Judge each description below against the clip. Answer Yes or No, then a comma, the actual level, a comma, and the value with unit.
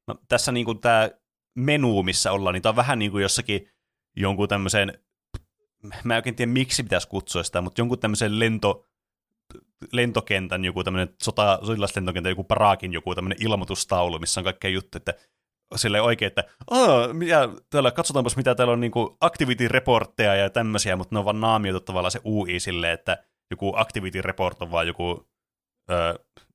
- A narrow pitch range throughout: No, average, 4.2 semitones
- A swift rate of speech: Yes, fast, 165 wpm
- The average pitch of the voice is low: Yes, low, 100 Hz